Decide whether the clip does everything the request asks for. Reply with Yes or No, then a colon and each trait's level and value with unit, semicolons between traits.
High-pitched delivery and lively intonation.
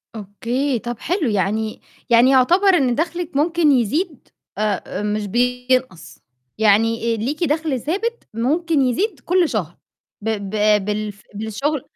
Yes: very high, 250 Hz; wide, 6.3 semitones